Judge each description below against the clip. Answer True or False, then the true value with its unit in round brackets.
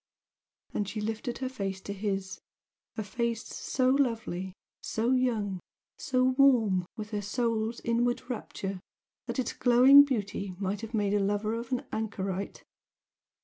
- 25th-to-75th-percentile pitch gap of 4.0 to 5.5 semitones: False (3.5 semitones)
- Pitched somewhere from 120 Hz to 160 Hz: False (220 Hz)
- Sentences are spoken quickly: False (145 wpm)